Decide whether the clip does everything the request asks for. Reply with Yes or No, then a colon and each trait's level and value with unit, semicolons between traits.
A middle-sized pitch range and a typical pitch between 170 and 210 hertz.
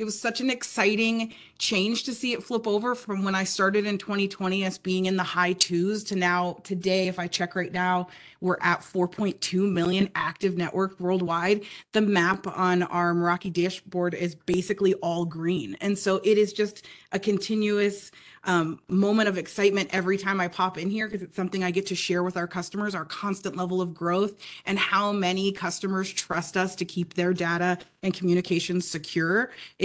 No: narrow, 2.1 semitones; high, 190 Hz